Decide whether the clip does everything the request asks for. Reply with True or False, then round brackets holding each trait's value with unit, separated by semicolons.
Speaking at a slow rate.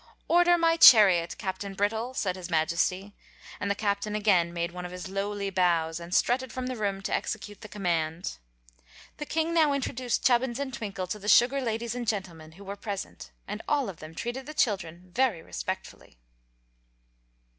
False (175 wpm)